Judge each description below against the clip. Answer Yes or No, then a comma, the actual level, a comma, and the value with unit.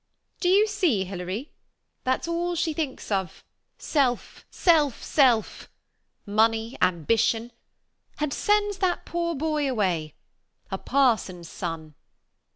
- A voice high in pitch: Yes, very high, 260 Hz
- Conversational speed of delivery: No, slow, 130 wpm